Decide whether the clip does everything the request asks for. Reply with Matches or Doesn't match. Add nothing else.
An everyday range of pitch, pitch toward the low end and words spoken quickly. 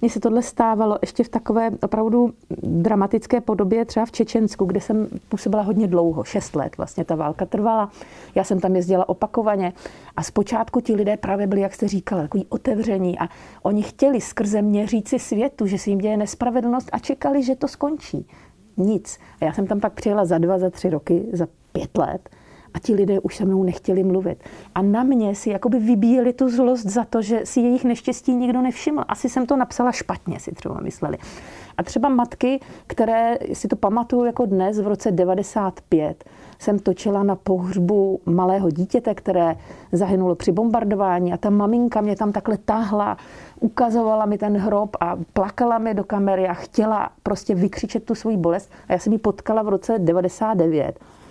Doesn't match